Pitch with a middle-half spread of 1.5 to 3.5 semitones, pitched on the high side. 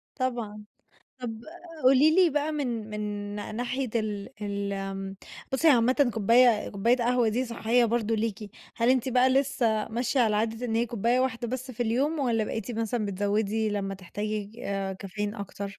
Yes: average, 3.1 semitones; high, 230 Hz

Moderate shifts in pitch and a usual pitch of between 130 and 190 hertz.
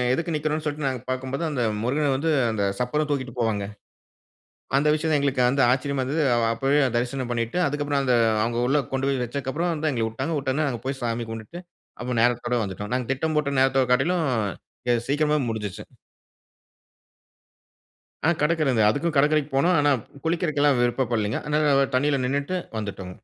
Yes: average, 3.6 semitones; low, 135 Hz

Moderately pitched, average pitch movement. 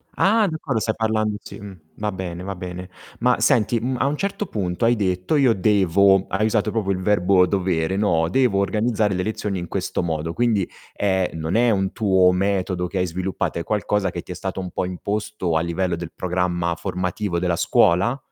No: very low, 95 Hz; average, 3.1 semitones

